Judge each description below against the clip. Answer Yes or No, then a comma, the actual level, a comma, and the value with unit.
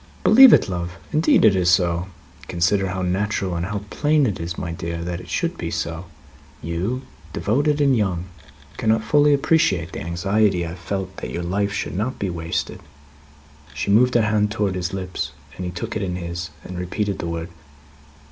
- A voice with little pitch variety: No, average, 3.7 semitones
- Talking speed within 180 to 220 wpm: Yes, average, 195 wpm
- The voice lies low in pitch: Yes, very low, 95 Hz